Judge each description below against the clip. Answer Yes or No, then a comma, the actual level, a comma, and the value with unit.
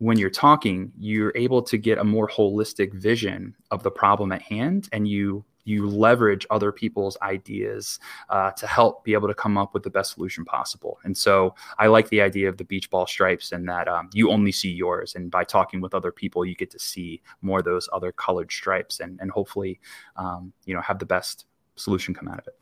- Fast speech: Yes, fast, 225 wpm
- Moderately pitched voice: No, low, 100 Hz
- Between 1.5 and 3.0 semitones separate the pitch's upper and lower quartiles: Yes, narrow, 2.4 semitones